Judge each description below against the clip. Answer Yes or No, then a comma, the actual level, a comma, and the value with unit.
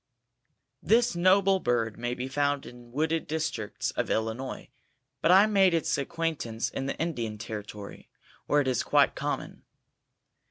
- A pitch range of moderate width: No, wide, 6.1 semitones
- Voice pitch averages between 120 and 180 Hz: Yes, medium, 140 Hz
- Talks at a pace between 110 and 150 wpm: Yes, average, 145 wpm